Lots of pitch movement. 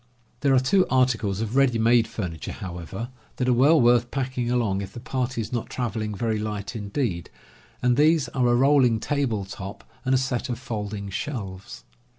No: average, 3.8 semitones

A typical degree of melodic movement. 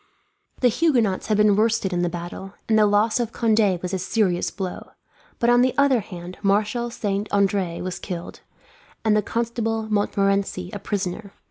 Yes: average, 3.0 semitones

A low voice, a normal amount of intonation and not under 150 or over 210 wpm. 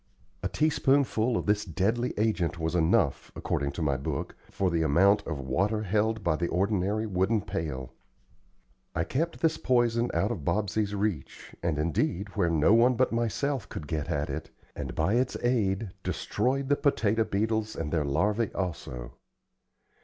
No: low, 100 Hz; wide, 5.7 semitones; average, 160 wpm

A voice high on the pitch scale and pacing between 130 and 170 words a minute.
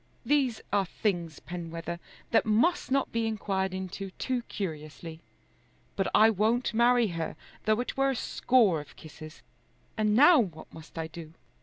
Yes: high, 200 Hz; average, 155 wpm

